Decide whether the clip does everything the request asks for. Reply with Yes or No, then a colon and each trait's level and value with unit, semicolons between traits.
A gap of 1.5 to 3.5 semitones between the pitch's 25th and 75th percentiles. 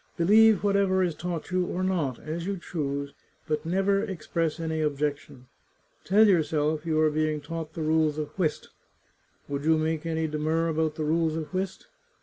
Yes: average, 2.8 semitones